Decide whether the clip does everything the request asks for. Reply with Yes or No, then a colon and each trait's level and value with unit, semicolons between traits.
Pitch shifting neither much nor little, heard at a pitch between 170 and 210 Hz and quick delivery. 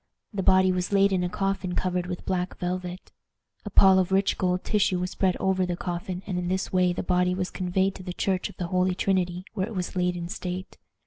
No: narrow, 1.0 semitones; medium, 185 Hz; fast, 235 wpm